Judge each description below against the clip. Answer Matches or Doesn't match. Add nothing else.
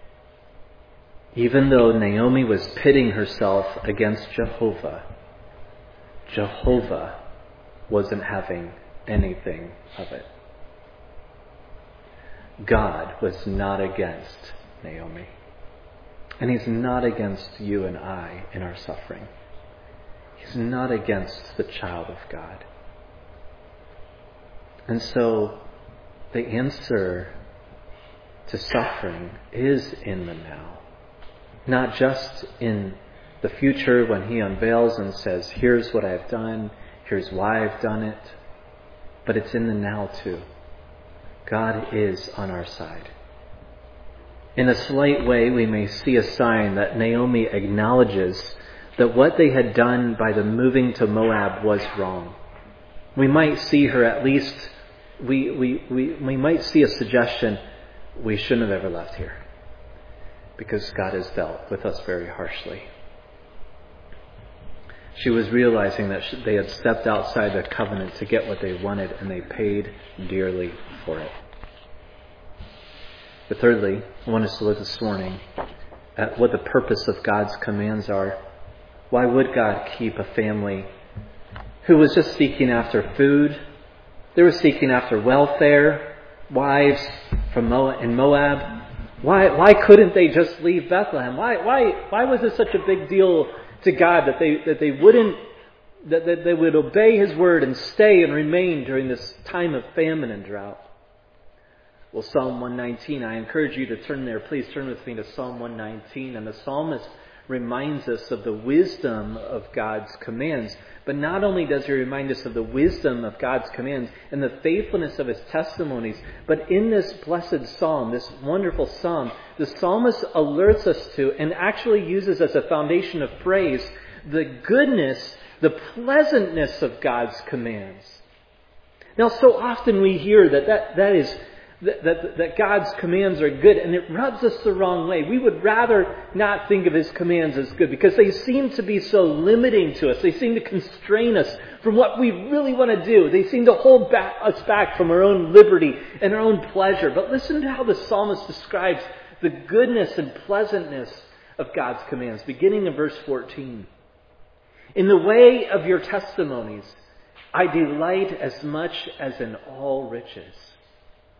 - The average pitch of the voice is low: Matches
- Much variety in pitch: Matches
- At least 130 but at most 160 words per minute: Matches